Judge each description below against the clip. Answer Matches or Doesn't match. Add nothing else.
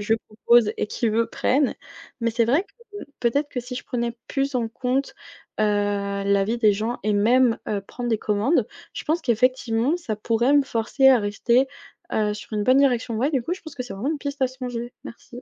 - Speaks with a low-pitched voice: Doesn't match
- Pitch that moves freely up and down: Doesn't match